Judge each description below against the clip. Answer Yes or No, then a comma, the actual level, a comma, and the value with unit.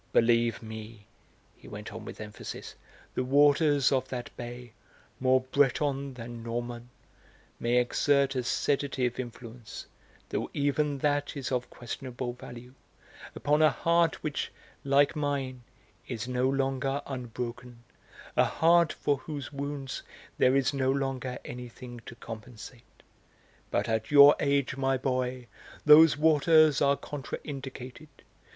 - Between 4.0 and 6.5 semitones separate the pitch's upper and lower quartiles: No, average, 2.7 semitones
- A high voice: No, low, 130 Hz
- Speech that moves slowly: Yes, slow, 130 wpm